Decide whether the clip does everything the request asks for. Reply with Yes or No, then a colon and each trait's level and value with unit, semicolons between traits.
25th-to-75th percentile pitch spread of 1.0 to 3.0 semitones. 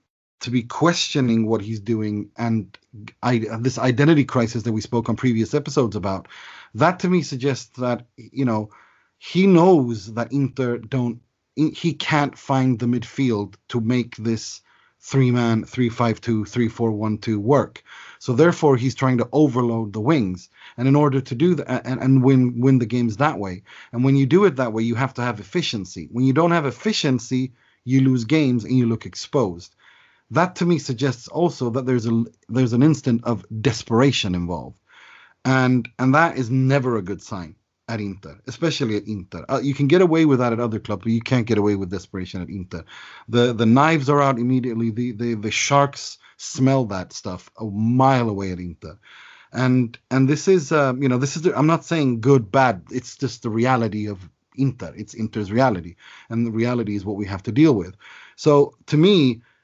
No: average, 3.5 semitones